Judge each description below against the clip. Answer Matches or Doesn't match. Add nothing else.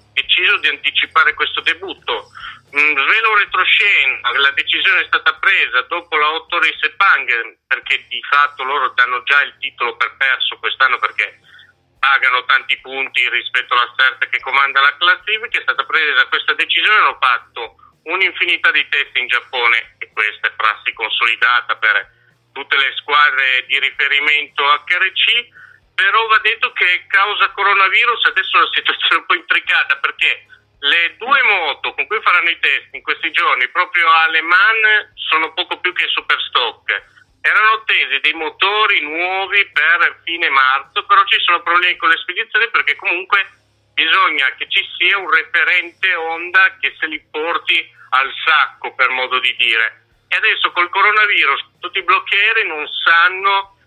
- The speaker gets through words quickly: Doesn't match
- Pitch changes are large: Matches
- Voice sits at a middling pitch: Matches